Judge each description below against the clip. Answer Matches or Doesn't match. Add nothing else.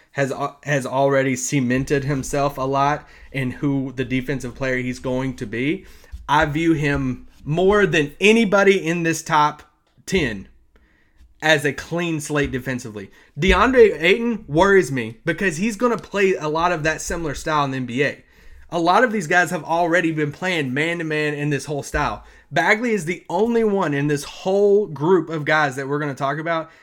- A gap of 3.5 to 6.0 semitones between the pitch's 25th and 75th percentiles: Matches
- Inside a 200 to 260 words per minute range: Doesn't match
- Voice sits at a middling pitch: Matches